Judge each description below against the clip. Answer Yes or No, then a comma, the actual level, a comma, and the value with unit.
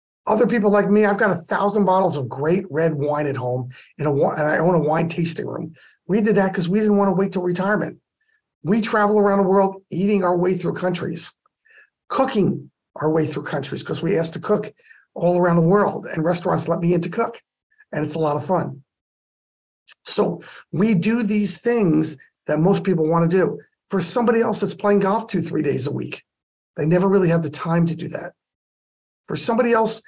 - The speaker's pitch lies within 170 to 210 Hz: Yes, medium, 185 Hz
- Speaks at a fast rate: Yes, fast, 210 wpm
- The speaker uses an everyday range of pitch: Yes, average, 4.4 semitones